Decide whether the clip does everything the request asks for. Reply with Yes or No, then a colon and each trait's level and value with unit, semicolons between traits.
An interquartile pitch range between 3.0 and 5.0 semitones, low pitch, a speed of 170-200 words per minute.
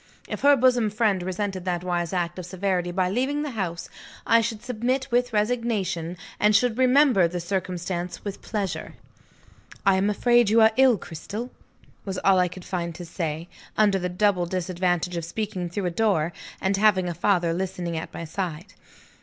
No: average, 3.9 semitones; high, 190 Hz; average, 180 wpm